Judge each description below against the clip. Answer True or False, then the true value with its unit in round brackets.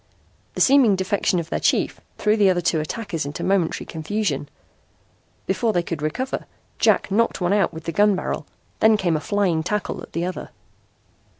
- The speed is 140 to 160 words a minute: False (180 wpm)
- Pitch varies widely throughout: False (4.3 semitones)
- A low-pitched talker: False (185 Hz)